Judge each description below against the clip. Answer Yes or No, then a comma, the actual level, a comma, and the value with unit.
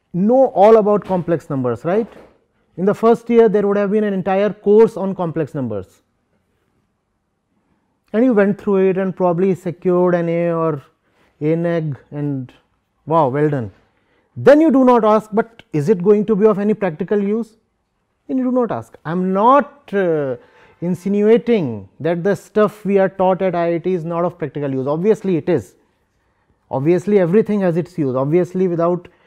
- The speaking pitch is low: No, medium, 185 Hz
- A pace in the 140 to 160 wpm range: No, average, 175 wpm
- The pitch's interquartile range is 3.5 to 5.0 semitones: Yes, average, 4.6 semitones